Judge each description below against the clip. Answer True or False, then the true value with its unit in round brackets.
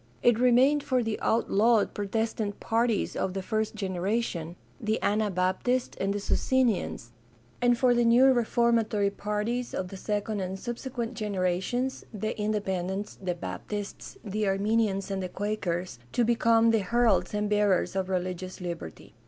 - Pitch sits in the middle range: False (210 Hz)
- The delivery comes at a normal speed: True (155 wpm)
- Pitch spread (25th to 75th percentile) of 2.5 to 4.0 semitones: True (3.6 semitones)